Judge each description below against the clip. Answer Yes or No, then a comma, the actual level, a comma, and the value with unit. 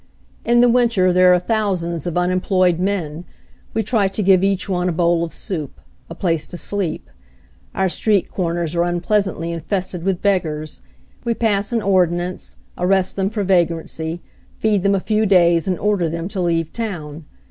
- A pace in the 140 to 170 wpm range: No, average, 180 wpm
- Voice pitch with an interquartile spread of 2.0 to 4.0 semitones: Yes, average, 2.8 semitones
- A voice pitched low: No, medium, 180 Hz